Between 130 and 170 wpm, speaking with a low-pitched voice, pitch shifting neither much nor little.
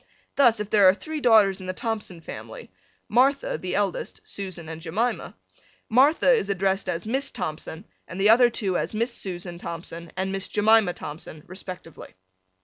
No: average, 165 wpm; high, 195 Hz; average, 4.2 semitones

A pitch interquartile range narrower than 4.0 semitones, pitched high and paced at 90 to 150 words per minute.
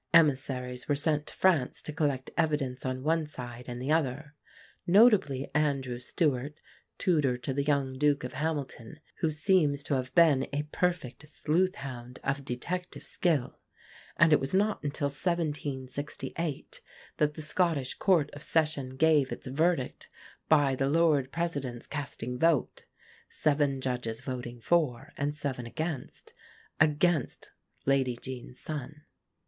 No: average, 3.4 semitones; medium, 145 Hz; average, 140 wpm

